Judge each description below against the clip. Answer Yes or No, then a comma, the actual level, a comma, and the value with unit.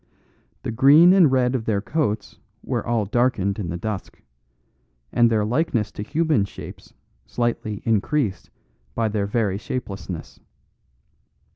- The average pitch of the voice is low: Yes, low, 110 Hz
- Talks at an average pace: No, slow, 130 wpm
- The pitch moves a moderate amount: Yes, average, 4.1 semitones